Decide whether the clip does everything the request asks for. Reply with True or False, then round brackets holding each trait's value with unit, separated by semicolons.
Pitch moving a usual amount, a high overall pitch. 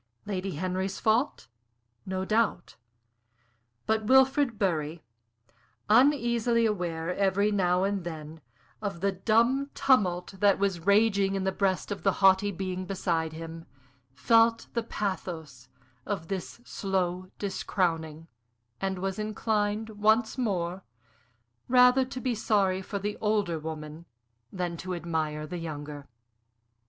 True (3.9 semitones; 195 Hz)